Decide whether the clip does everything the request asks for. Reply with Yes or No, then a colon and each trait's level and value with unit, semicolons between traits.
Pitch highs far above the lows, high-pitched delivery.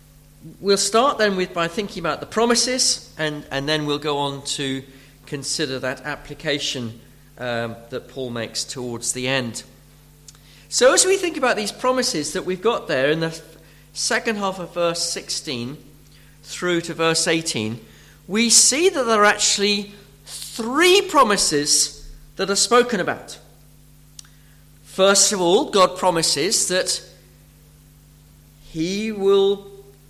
No: wide, 6.0 semitones; medium, 155 Hz